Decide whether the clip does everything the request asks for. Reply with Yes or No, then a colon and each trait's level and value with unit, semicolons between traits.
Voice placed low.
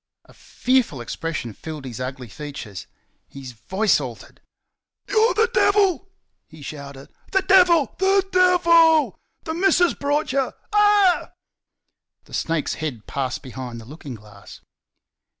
No: medium, 180 Hz